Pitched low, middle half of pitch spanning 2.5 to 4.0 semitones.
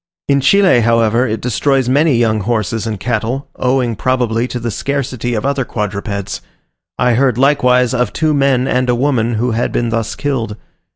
Yes: low, 125 Hz; average, 2.8 semitones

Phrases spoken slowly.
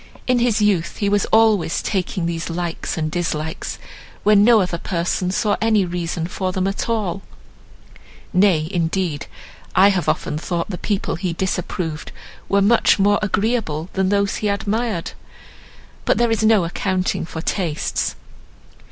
No: average, 145 wpm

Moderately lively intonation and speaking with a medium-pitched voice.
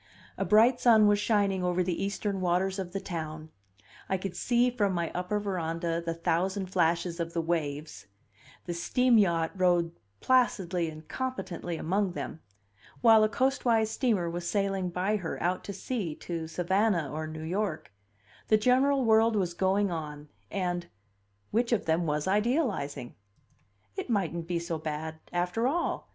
Yes: average, 4.1 semitones; medium, 180 Hz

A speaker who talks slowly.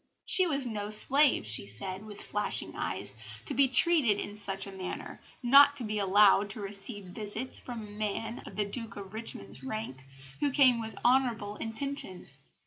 No: average, 175 wpm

